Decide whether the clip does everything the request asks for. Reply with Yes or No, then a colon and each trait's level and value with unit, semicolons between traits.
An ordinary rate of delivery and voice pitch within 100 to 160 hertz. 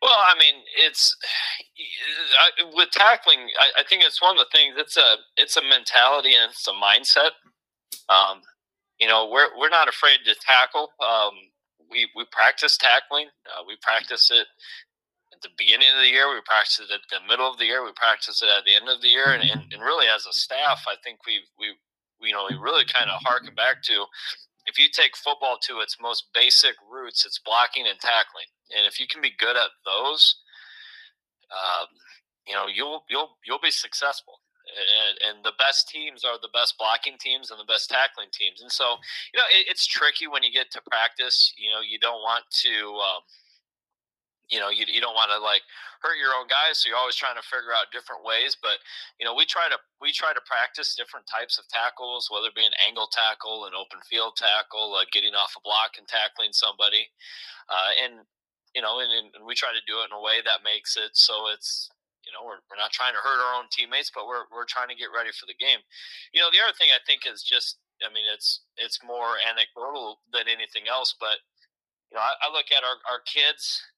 No: fast, 220 wpm; medium, 140 Hz